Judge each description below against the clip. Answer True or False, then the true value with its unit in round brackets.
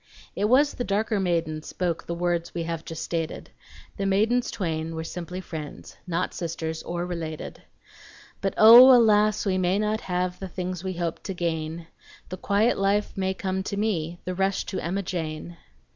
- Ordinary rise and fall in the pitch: True (3.0 semitones)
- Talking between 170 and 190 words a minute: True (175 wpm)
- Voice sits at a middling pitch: True (180 Hz)